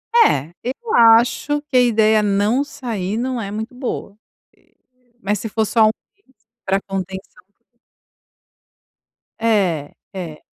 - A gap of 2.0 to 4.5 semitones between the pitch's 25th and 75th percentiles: Yes, average, 4.0 semitones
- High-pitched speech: Yes, high, 215 Hz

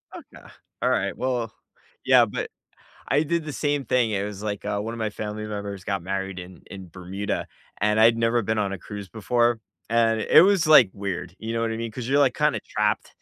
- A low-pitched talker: Yes, low, 110 Hz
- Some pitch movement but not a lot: Yes, average, 3.0 semitones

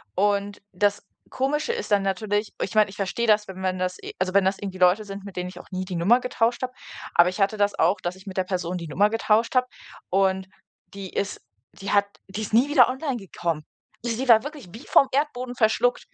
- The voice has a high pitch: Yes, high, 200 Hz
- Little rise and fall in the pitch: No, average, 3.6 semitones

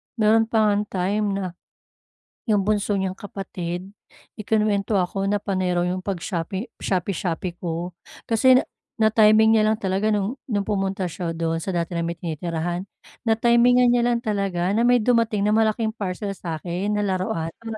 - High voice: Yes, high, 200 Hz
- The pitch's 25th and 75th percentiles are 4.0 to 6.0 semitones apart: No, average, 3.3 semitones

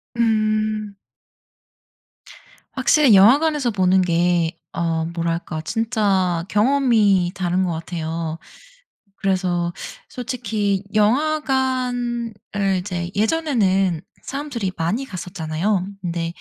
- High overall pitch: Yes, high, 200 Hz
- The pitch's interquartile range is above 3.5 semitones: Yes, wide, 5.4 semitones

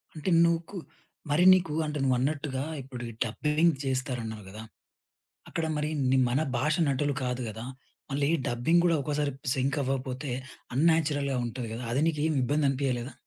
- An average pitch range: Yes, average, 3.0 semitones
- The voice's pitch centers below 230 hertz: Yes, medium, 140 Hz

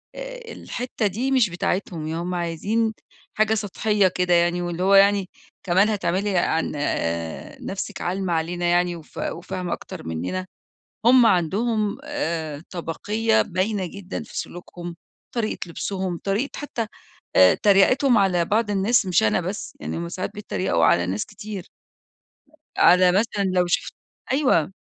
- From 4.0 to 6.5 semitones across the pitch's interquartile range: No, average, 3.6 semitones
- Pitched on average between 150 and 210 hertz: Yes, high, 190 Hz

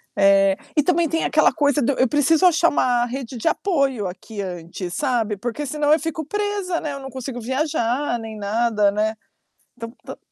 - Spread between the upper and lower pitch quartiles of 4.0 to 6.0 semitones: Yes, wide, 5.5 semitones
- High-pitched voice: Yes, very high, 260 Hz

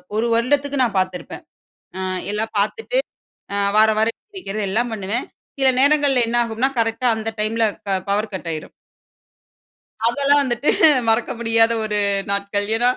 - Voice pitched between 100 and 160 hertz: No, high, 225 Hz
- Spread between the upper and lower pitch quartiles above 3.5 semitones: No, average, 3.2 semitones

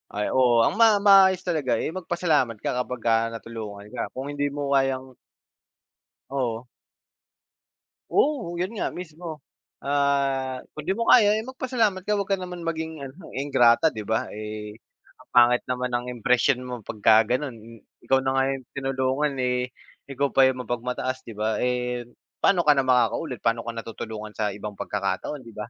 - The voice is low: Yes, low, 130 Hz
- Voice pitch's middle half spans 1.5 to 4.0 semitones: No, average, 4.8 semitones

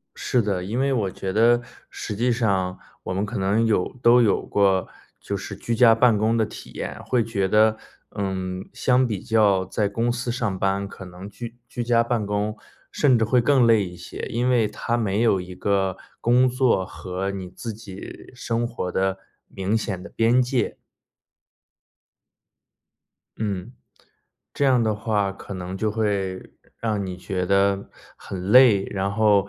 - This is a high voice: No, low, 105 Hz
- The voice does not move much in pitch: No, average, 3.4 semitones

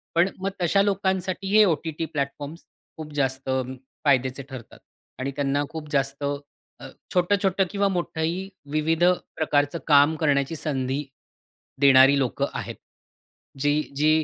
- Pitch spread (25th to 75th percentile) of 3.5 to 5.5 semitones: Yes, average, 3.9 semitones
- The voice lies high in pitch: No, medium, 150 Hz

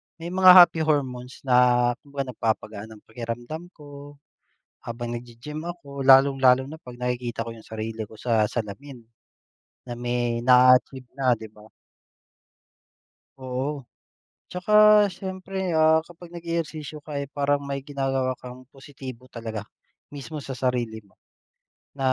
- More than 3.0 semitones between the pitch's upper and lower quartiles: Yes, average, 3.4 semitones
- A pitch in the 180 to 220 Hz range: No, low, 130 Hz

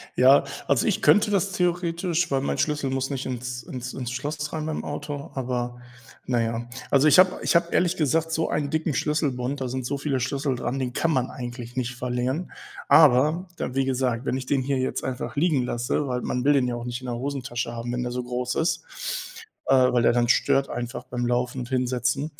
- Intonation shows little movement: No, average, 3.4 semitones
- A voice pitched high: No, low, 130 Hz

